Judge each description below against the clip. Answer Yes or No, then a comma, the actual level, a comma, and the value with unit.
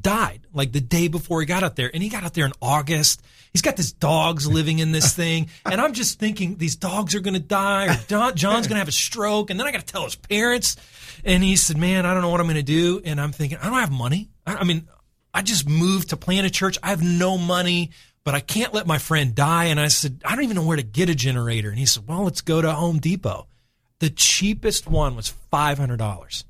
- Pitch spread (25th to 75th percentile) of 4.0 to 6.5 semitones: Yes, average, 4.3 semitones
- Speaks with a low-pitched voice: No, medium, 165 Hz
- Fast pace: Yes, fast, 260 wpm